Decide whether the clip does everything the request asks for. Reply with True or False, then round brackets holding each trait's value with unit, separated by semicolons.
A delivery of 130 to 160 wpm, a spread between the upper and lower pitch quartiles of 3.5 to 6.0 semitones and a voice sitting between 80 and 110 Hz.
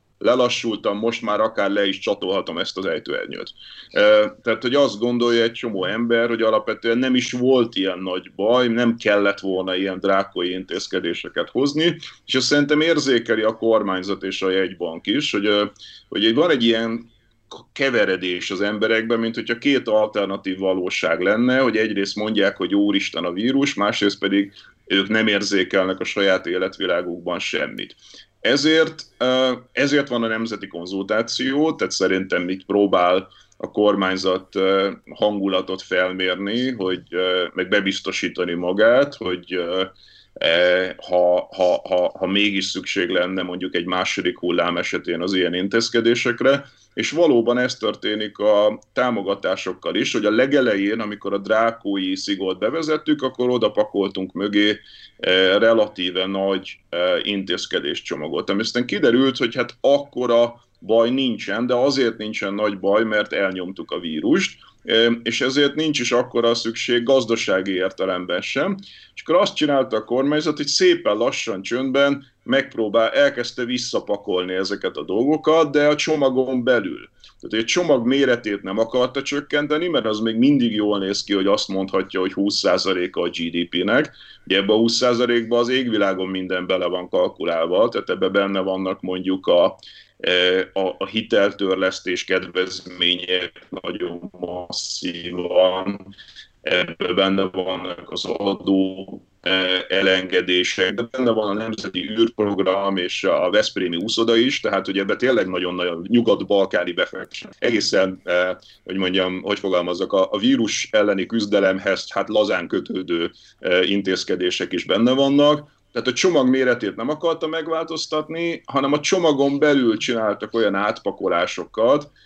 True (135 wpm; 4.7 semitones; 105 Hz)